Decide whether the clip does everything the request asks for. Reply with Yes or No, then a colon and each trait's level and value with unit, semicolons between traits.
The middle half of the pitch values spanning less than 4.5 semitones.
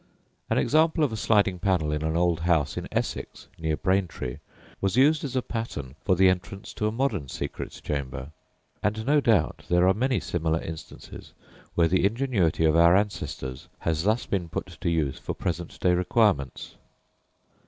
No: average, 5.2 semitones